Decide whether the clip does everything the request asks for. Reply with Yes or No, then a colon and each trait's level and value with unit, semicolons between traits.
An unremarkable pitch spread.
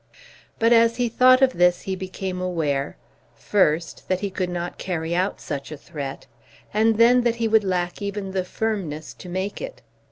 Yes: average, 4.2 semitones